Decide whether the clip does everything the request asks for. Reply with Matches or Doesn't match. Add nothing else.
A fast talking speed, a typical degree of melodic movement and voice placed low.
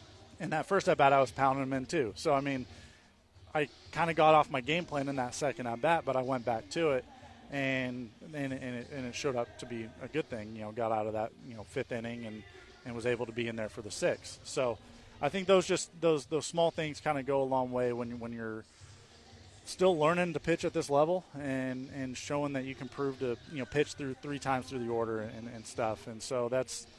Matches